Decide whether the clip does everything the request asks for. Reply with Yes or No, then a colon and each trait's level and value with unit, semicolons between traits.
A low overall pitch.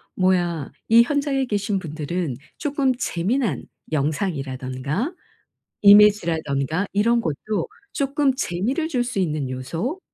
No: high, 190 Hz